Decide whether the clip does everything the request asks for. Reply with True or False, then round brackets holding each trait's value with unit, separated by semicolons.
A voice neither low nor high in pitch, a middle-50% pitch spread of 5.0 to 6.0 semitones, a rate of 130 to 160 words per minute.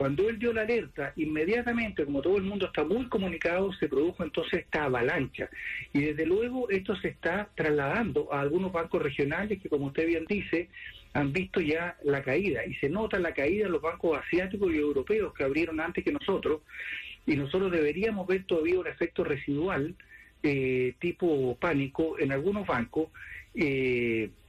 False (165 Hz; 5.5 semitones; 170 wpm)